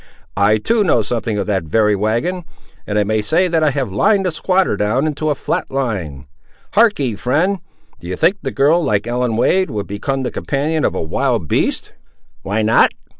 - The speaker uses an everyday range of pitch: No, wide, 7.2 semitones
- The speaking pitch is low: Yes, low, 125 Hz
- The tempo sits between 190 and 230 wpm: Yes, average, 195 wpm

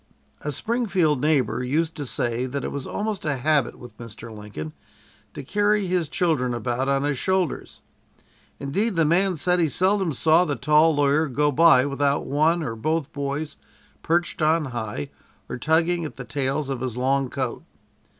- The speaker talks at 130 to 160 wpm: No, average, 170 wpm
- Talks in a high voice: No, medium, 145 Hz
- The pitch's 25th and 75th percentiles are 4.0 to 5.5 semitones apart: Yes, average, 4.3 semitones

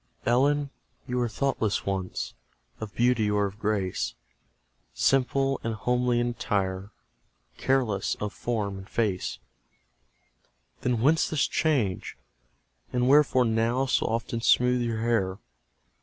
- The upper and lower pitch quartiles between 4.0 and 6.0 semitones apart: No, average, 3.3 semitones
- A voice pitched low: Yes, low, 115 Hz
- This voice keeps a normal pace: No, slow, 120 wpm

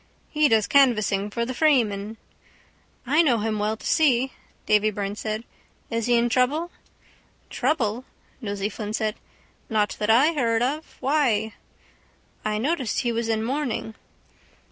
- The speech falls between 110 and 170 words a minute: Yes, average, 145 wpm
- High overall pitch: Yes, high, 230 Hz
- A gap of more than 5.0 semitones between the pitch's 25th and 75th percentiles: No, average, 3.8 semitones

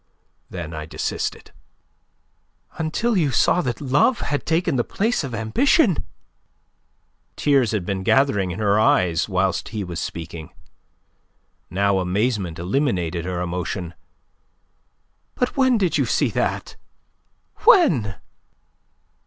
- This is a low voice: Yes, low, 105 Hz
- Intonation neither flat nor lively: No, wide, 8.5 semitones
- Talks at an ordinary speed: No, slow, 115 wpm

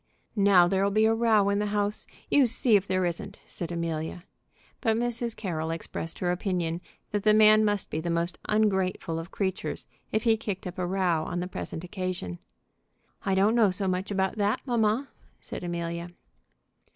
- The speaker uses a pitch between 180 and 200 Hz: Yes, high, 190 Hz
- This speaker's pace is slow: No, average, 180 wpm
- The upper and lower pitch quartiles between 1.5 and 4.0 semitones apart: Yes, average, 3.4 semitones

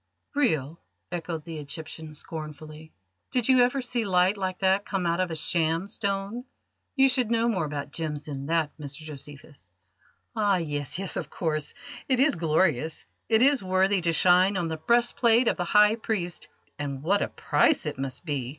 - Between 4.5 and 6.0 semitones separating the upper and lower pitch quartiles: Yes, average, 5.3 semitones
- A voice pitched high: No, medium, 175 Hz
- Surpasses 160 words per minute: Yes, average, 180 wpm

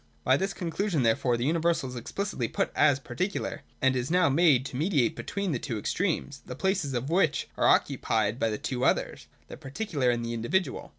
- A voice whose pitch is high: No, medium, 140 Hz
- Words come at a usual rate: No, fast, 210 wpm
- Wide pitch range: Yes, wide, 6.2 semitones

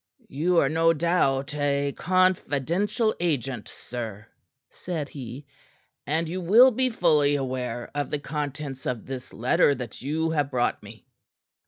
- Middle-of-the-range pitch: Yes, medium, 145 Hz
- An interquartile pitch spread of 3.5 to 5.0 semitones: Yes, average, 4.0 semitones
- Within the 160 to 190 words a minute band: No, average, 140 wpm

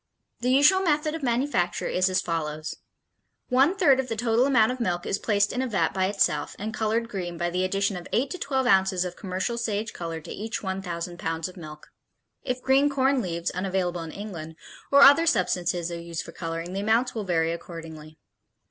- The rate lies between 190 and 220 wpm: Yes, average, 200 wpm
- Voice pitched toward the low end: No, high, 195 Hz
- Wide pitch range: Yes, wide, 6.2 semitones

